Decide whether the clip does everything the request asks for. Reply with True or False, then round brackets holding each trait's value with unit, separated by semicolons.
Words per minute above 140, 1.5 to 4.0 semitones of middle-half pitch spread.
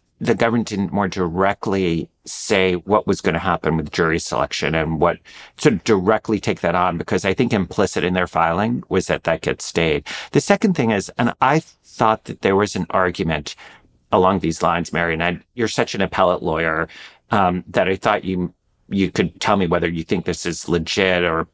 True (205 wpm; 3.3 semitones)